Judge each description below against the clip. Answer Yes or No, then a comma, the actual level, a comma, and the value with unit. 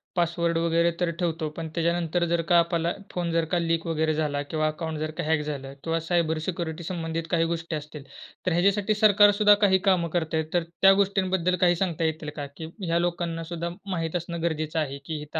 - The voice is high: No, medium, 165 Hz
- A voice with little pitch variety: Yes, narrow, 1.7 semitones